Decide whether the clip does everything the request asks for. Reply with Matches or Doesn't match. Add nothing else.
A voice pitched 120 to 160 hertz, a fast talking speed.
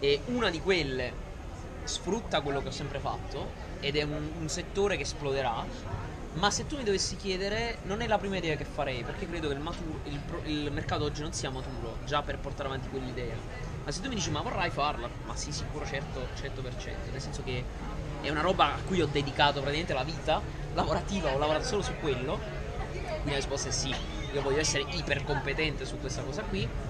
Matches